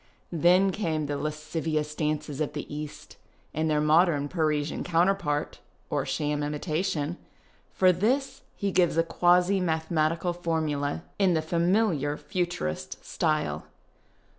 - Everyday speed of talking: No, slow, 125 wpm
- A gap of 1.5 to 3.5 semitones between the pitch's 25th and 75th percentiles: Yes, average, 2.9 semitones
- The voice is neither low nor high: Yes, medium, 160 Hz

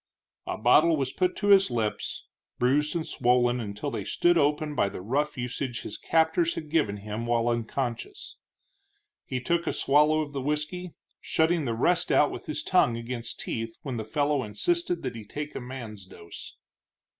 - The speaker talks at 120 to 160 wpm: No, average, 175 wpm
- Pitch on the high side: No, low, 135 Hz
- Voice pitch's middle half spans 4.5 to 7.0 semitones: Yes, average, 5.1 semitones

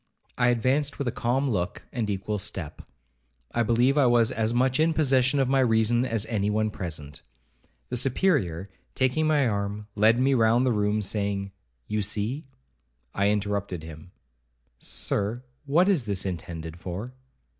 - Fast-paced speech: No, average, 155 wpm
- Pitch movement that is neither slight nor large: Yes, average, 4.6 semitones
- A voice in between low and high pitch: No, low, 110 Hz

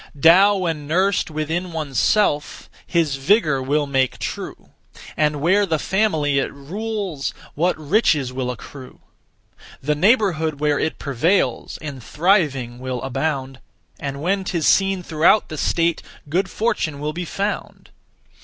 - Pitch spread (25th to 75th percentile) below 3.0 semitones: No, average, 4.9 semitones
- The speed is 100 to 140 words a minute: Yes, slow, 135 wpm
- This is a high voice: No, medium, 155 Hz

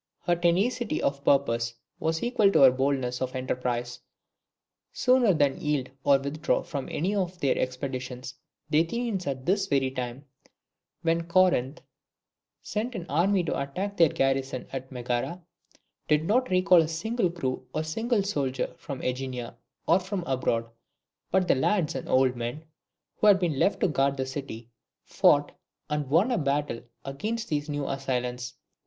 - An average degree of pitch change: No, wide, 5.8 semitones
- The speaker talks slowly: No, average, 160 wpm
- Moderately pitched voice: Yes, medium, 145 Hz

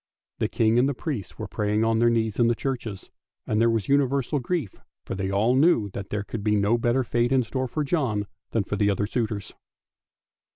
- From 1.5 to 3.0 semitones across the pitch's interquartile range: No, average, 3.8 semitones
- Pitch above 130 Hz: No, low, 115 Hz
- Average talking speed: No, fast, 215 wpm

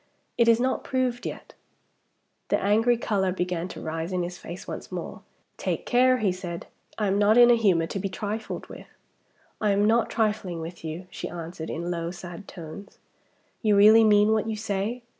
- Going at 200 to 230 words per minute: No, average, 190 wpm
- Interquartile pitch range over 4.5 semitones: No, average, 4.0 semitones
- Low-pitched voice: No, high, 200 Hz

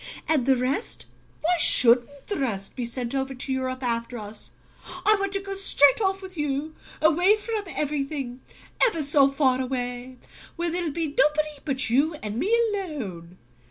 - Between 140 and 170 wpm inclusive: Yes, average, 165 wpm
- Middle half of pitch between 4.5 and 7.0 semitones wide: Yes, average, 5.0 semitones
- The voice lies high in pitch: Yes, very high, 280 Hz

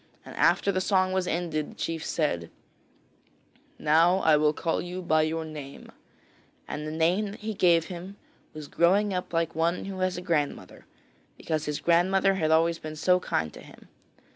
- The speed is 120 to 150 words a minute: No, average, 180 wpm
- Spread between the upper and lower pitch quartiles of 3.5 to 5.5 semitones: No, average, 3.0 semitones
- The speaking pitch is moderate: Yes, medium, 170 Hz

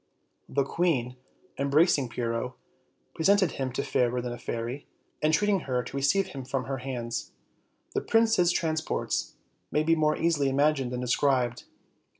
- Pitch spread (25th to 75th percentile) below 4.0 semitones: No, average, 4.4 semitones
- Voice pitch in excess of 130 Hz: Yes, medium, 140 Hz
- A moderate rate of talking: Yes, average, 145 wpm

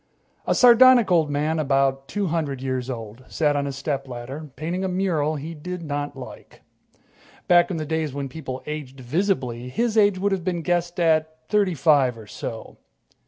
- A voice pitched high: No, medium, 155 Hz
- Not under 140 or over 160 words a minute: No, average, 175 wpm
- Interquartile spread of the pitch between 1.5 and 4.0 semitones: No, average, 4.5 semitones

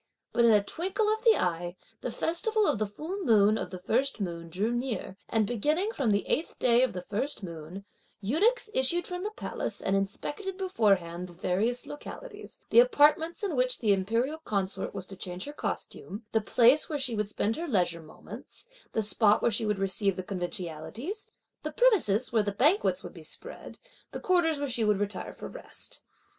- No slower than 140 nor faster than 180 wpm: No, average, 195 wpm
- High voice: Yes, high, 225 Hz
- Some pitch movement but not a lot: No, wide, 8.2 semitones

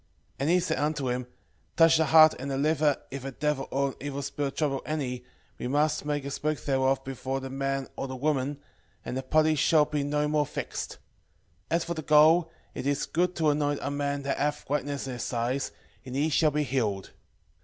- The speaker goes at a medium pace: No, fast, 220 wpm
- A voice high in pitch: No, medium, 145 Hz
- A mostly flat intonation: Yes, narrow, 2.2 semitones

